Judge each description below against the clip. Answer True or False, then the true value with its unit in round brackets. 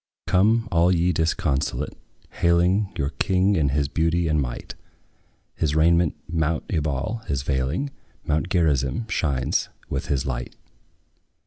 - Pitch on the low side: True (80 Hz)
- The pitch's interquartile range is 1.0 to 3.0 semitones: False (4.0 semitones)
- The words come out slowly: True (125 wpm)